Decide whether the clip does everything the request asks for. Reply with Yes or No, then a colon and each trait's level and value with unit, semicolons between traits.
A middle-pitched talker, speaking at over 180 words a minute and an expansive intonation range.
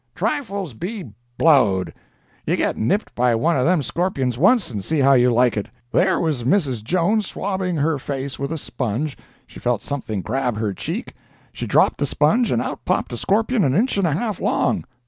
Yes: medium, 145 Hz; average, 190 wpm; wide, 7.1 semitones